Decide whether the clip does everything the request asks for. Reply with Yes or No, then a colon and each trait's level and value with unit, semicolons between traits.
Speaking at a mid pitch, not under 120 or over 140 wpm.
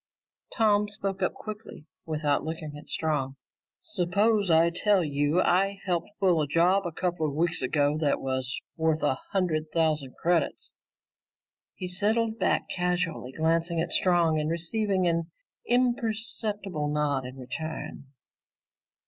Yes: medium, 170 Hz; slow, 135 wpm